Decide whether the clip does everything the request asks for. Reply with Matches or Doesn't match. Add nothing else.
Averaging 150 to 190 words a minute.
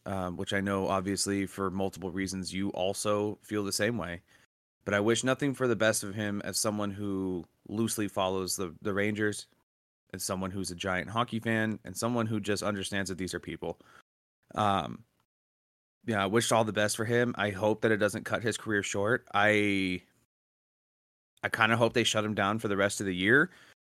Doesn't match